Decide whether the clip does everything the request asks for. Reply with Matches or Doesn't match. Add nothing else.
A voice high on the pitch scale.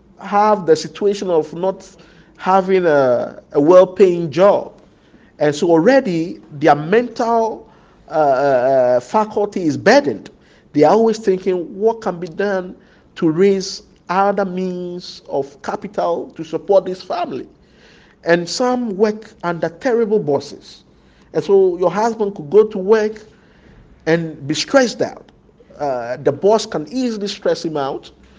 Matches